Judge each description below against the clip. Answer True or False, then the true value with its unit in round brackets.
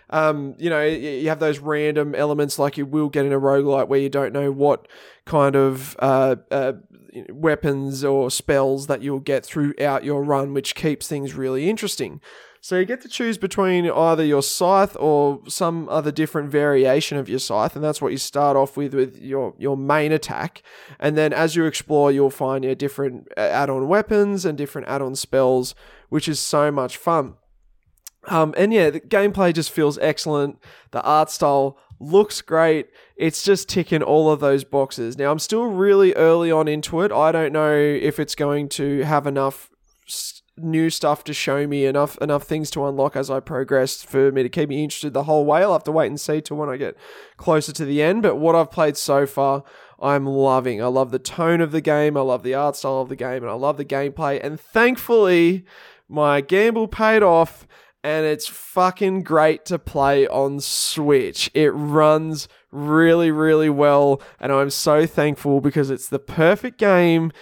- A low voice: False (145 Hz)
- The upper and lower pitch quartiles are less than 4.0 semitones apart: True (2.6 semitones)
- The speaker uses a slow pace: False (195 wpm)